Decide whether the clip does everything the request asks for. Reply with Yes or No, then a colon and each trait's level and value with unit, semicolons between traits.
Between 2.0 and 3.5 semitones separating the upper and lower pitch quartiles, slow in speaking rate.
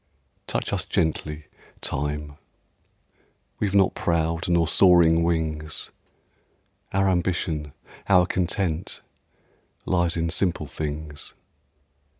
Yes: average, 2.7 semitones; slow, 90 wpm